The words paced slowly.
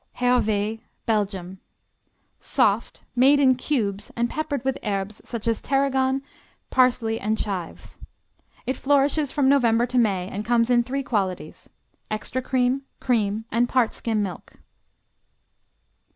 Yes: slow, 125 wpm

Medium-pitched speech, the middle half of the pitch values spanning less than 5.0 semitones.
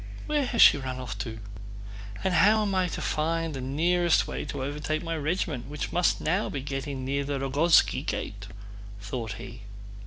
Yes: medium, 150 Hz; average, 4.5 semitones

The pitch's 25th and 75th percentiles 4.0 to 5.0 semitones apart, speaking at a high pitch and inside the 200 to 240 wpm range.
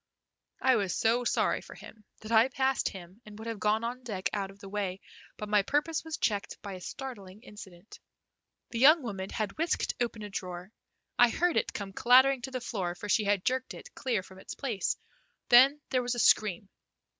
Yes: average, 4.4 semitones; high, 220 Hz; fast, 205 wpm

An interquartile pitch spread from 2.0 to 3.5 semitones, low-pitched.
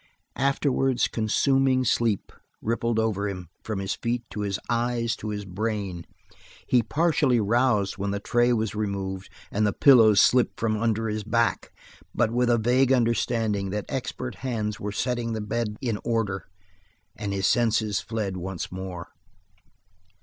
Yes: average, 2.9 semitones; low, 110 Hz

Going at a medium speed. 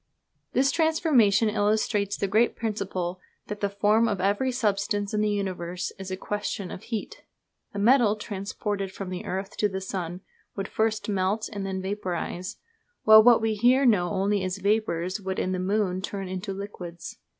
Yes: average, 170 wpm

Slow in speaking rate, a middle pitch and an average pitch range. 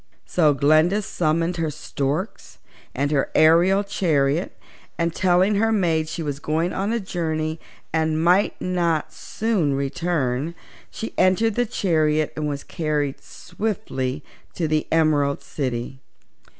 Yes: slow, 130 wpm; medium, 160 Hz; average, 3.4 semitones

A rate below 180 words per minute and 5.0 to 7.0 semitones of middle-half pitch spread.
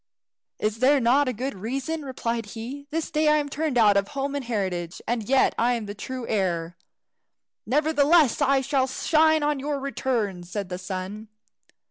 Yes: average, 170 wpm; wide, 5.4 semitones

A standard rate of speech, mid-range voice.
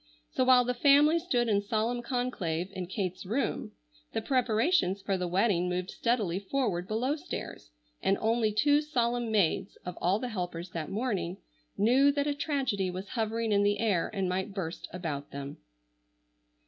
No: average, 165 wpm; high, 215 Hz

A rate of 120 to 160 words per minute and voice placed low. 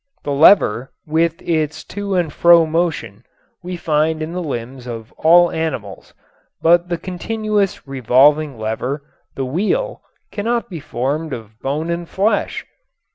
No: average, 140 wpm; medium, 160 Hz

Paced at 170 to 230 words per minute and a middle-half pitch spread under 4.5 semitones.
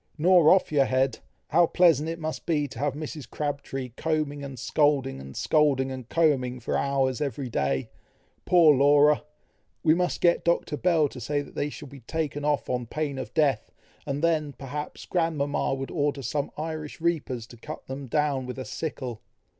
Yes: average, 180 wpm; average, 2.8 semitones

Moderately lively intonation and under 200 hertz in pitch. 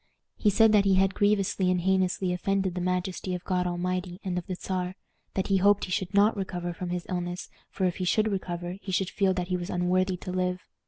No: narrow, 1.3 semitones; medium, 185 Hz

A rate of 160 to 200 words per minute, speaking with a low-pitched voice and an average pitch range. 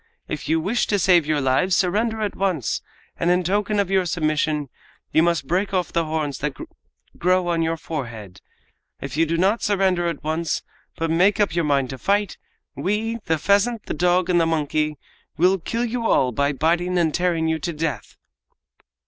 No: average, 190 wpm; medium, 170 Hz; average, 3.7 semitones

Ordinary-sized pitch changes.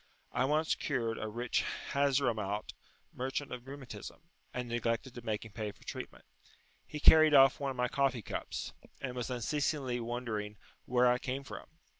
Yes: average, 3.0 semitones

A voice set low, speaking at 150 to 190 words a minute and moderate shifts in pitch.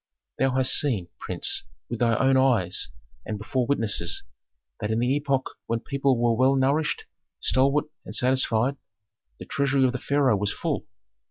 Yes: low, 130 Hz; average, 160 wpm; average, 3.1 semitones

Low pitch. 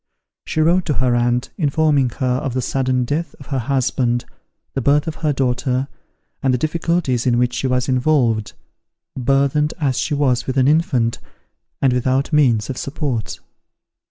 Yes: low, 130 Hz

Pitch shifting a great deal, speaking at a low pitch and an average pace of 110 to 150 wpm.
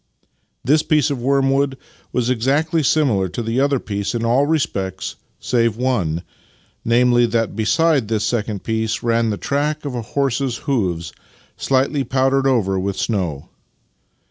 No: average, 4.1 semitones; low, 120 Hz; average, 145 wpm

